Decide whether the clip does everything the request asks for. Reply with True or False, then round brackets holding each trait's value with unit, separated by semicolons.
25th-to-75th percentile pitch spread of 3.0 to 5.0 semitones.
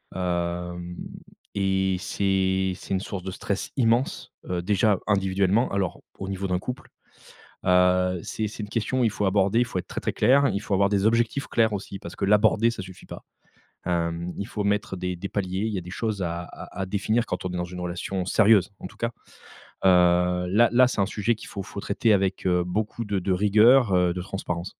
False (2.6 semitones)